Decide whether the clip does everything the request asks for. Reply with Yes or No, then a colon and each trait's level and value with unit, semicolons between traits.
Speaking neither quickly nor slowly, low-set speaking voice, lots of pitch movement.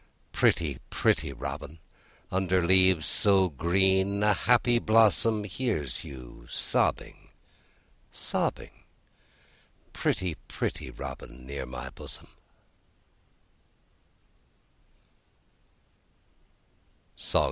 No: slow, 70 wpm; very low, 95 Hz; wide, 6.1 semitones